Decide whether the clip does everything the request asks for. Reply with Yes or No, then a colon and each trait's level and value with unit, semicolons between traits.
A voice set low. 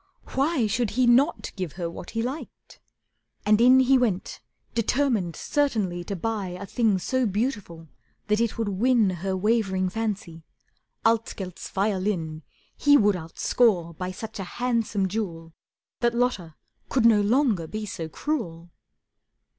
No: high, 210 Hz